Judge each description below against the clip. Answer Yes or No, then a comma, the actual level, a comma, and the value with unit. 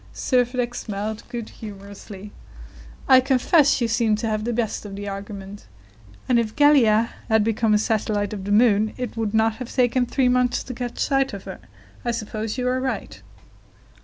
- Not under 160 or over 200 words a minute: Yes, average, 180 wpm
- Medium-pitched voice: No, high, 225 Hz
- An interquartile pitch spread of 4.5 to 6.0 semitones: No, average, 2.9 semitones